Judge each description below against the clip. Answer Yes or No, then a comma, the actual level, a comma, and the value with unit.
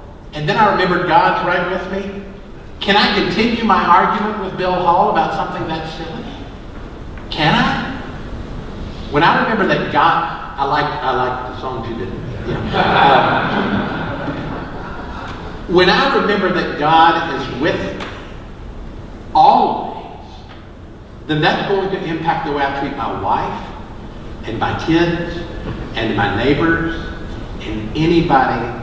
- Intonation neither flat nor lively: No, wide, 7.4 semitones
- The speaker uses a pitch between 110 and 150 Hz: No, medium, 160 Hz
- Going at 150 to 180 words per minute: No, slow, 135 wpm